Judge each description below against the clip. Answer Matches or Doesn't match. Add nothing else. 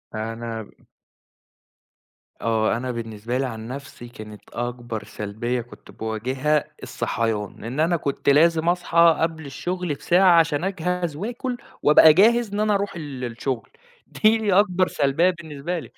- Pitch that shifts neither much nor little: Doesn't match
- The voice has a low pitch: Doesn't match